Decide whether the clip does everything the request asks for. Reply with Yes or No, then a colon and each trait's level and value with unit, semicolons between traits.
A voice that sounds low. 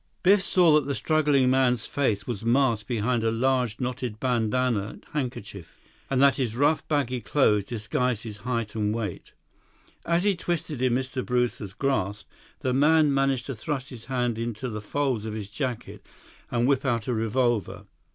Yes: low, 125 Hz